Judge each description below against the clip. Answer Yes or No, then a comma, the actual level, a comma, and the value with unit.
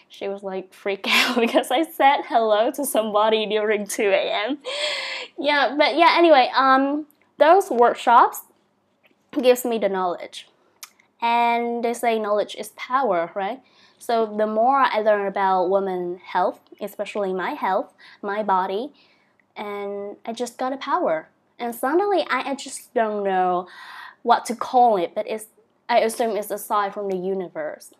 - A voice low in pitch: No, high, 235 Hz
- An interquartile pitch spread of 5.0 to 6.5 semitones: Yes, average, 5.3 semitones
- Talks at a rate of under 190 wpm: Yes, average, 155 wpm